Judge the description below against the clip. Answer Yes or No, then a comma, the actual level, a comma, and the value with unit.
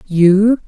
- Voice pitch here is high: Yes, high, 200 Hz